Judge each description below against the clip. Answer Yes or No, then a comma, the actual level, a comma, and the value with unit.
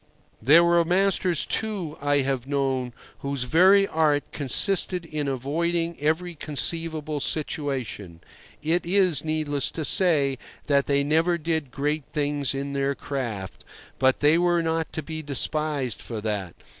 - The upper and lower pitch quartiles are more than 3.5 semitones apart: No, average, 3.2 semitones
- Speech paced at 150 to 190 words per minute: No, average, 140 wpm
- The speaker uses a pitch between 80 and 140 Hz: No, medium, 150 Hz